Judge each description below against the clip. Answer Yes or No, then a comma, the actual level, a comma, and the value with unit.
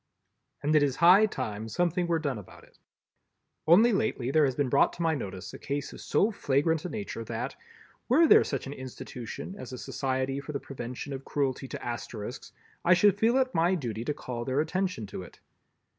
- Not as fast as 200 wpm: No, fast, 205 wpm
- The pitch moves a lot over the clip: Yes, wide, 5.7 semitones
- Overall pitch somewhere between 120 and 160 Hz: Yes, medium, 140 Hz